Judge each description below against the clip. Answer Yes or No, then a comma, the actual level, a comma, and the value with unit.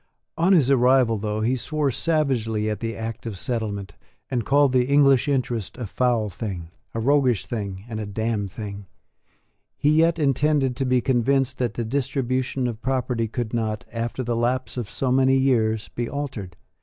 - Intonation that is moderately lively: Yes, average, 3.4 semitones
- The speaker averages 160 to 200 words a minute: Yes, average, 175 wpm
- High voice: No, low, 120 Hz